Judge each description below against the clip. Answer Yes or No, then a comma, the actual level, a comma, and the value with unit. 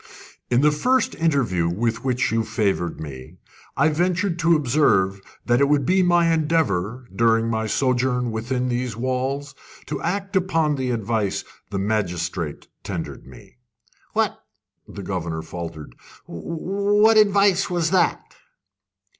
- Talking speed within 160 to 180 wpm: No, slow, 135 wpm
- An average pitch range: No, wide, 8.2 semitones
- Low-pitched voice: Yes, low, 125 Hz